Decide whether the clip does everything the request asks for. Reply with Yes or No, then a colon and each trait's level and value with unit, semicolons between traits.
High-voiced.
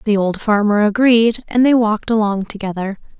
Yes: high, 215 Hz